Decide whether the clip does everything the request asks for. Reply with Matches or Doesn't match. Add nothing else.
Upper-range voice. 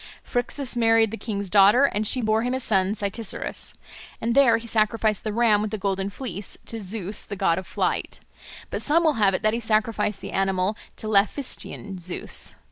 Matches